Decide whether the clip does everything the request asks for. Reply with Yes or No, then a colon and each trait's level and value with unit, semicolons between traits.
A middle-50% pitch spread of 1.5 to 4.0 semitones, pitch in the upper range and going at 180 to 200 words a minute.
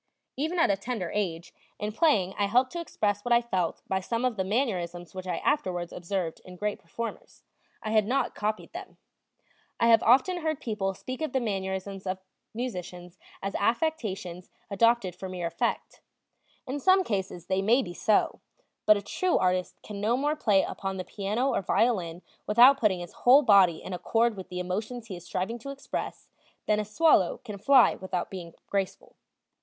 No: average, 4.7 semitones; high, 205 Hz; average, 185 wpm